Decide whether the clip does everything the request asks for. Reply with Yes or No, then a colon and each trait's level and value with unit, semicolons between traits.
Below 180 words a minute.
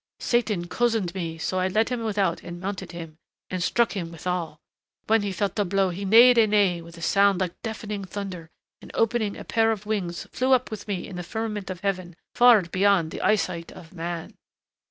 No: fast, 205 wpm